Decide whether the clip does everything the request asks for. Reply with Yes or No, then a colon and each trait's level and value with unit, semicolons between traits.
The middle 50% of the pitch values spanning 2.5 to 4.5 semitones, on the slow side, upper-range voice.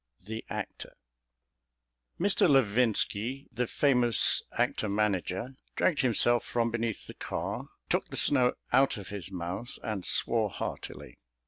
No: average, 3.7 semitones; slow, 130 wpm; low, 115 Hz